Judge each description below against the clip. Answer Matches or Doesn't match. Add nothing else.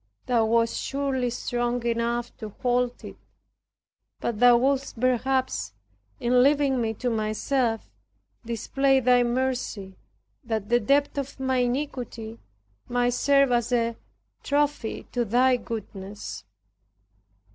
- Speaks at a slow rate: Matches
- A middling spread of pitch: Doesn't match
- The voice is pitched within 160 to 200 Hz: Doesn't match